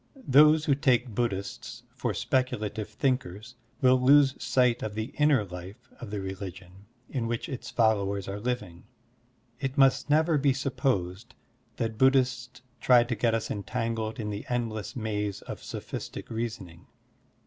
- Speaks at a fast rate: No, average, 150 wpm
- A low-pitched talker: Yes, low, 115 Hz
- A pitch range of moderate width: Yes, average, 4.1 semitones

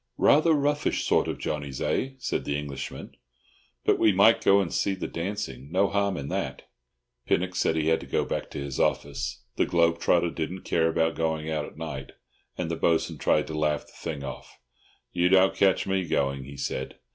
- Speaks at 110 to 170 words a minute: No, average, 195 wpm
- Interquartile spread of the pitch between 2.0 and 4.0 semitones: No, average, 4.5 semitones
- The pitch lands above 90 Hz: No, very low, 80 Hz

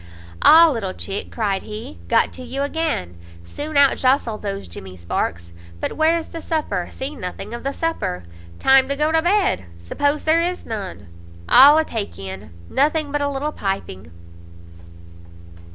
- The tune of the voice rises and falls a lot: Yes, wide, 8.0 semitones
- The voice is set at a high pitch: Yes, very high, 265 Hz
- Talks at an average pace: Yes, average, 160 wpm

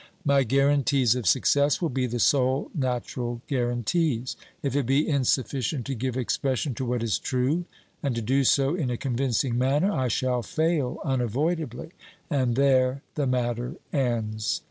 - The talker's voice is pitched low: Yes, low, 130 Hz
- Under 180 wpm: Yes, average, 155 wpm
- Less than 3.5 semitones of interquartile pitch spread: Yes, narrow, 2.5 semitones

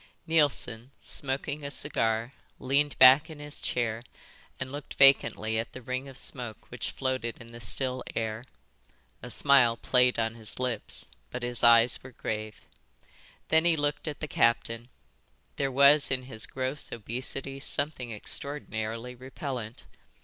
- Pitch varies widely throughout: No, average, 3.2 semitones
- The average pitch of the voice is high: No, low, 130 Hz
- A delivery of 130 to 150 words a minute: Yes, average, 145 wpm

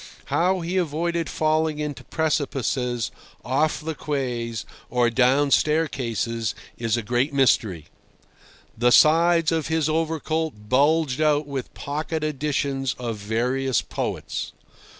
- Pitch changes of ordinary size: Yes, average, 4.3 semitones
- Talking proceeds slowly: Yes, slow, 115 wpm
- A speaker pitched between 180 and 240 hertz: No, medium, 140 Hz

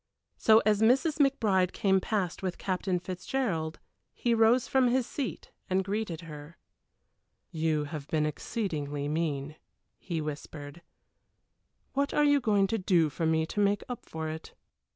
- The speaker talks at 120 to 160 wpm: Yes, average, 150 wpm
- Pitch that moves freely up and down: Yes, wide, 5.9 semitones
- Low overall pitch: No, medium, 185 Hz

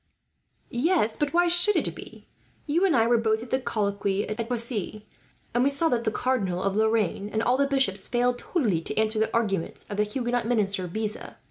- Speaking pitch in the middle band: No, high, 230 Hz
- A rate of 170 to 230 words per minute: Yes, fast, 205 wpm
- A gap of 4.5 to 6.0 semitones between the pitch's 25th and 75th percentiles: No, average, 3.6 semitones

